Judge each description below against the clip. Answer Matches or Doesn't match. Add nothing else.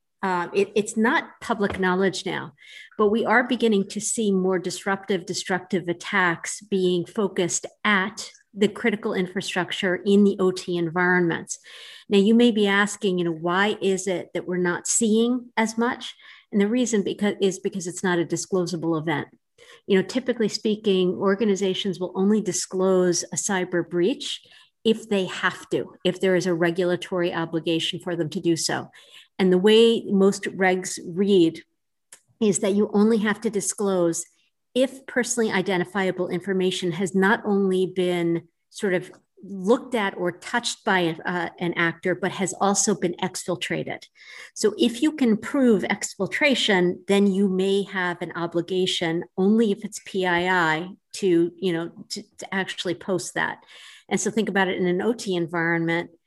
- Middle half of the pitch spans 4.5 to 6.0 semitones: Doesn't match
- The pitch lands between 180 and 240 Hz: Matches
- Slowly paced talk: Doesn't match